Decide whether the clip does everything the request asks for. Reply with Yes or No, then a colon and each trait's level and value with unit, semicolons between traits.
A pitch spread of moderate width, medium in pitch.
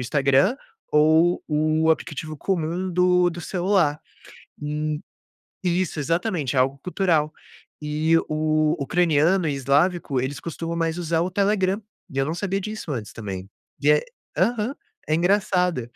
Yes: average, 3.3 semitones; medium, 165 Hz